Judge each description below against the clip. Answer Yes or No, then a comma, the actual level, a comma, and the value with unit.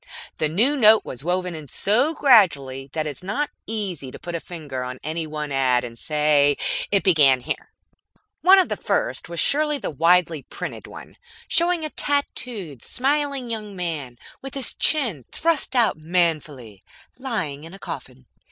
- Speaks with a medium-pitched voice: Yes, medium, 170 Hz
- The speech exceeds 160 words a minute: Yes, average, 170 wpm